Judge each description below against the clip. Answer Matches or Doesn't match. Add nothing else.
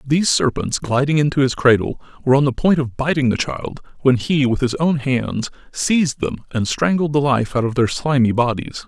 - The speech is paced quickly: Matches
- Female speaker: Doesn't match